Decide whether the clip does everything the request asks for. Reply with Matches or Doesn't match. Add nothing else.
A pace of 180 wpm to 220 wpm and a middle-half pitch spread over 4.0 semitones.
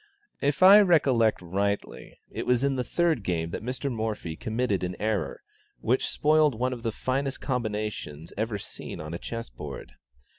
Doesn't match